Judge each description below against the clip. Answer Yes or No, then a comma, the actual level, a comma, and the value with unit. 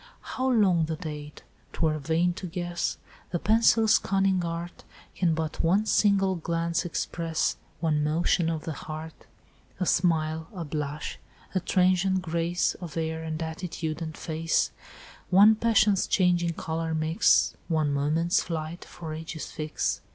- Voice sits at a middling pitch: Yes, medium, 165 Hz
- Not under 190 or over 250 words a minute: No, average, 140 wpm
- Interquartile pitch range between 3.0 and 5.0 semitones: No, narrow, 2.4 semitones